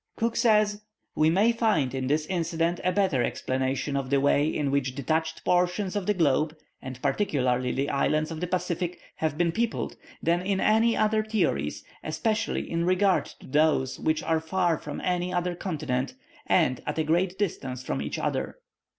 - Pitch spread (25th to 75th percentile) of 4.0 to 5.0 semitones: Yes, average, 4.7 semitones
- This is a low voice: No, medium, 165 Hz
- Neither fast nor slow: Yes, average, 175 wpm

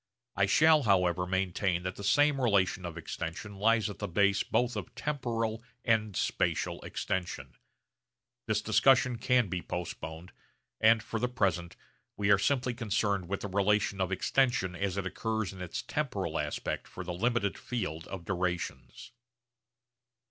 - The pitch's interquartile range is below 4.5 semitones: Yes, average, 3.9 semitones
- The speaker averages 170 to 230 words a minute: No, average, 150 wpm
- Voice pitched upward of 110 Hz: No, low, 100 Hz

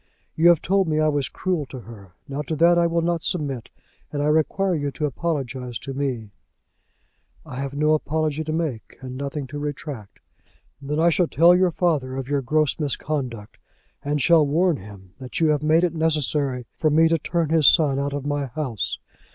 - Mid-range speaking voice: Yes, medium, 150 Hz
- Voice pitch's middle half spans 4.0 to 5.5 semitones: No, average, 3.2 semitones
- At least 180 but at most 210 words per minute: Yes, average, 200 wpm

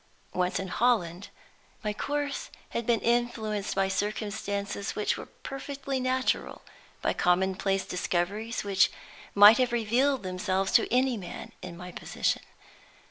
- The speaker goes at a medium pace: No, slow, 130 wpm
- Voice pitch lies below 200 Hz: No, high, 210 Hz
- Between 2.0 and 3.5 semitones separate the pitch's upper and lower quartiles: No, average, 4.1 semitones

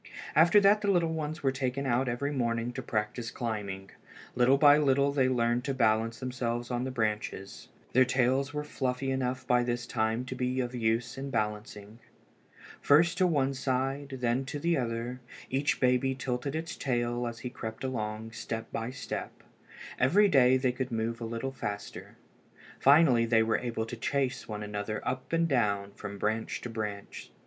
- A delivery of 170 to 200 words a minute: Yes, average, 175 wpm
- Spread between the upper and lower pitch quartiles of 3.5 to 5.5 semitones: No, average, 3.0 semitones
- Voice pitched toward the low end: Yes, low, 125 Hz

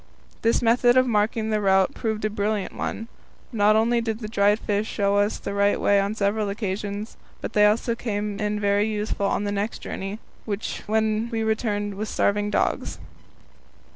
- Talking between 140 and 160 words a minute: No, average, 175 wpm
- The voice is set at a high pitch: Yes, high, 210 Hz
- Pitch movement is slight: Yes, narrow, 1.4 semitones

